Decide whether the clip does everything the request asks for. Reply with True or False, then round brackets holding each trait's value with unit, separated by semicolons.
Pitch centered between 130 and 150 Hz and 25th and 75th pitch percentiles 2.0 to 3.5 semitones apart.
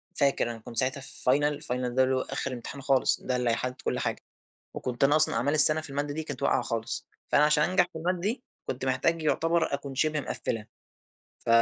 True (140 Hz; 3.1 semitones)